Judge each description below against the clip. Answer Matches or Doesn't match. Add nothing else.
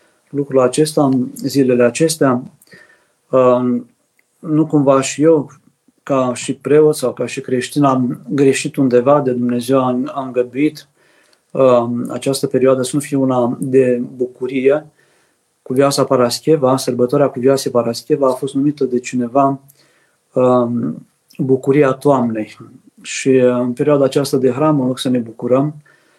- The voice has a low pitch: Matches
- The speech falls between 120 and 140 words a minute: Matches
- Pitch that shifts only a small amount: Matches